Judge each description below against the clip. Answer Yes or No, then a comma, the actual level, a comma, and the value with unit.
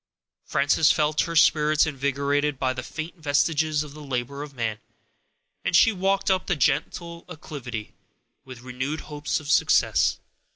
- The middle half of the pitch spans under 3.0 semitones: Yes, narrow, 2.5 semitones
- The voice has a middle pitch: Yes, medium, 150 Hz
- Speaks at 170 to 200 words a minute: No, average, 150 wpm